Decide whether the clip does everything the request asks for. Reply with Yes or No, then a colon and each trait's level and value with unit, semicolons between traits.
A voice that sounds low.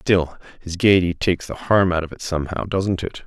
Yes: very low, 90 Hz